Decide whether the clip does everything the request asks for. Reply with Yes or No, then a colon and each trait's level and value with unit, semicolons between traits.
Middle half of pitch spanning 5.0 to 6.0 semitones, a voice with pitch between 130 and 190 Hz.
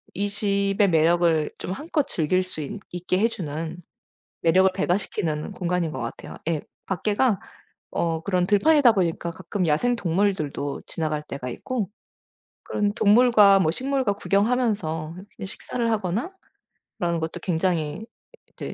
No: average, 4.1 semitones; medium, 185 Hz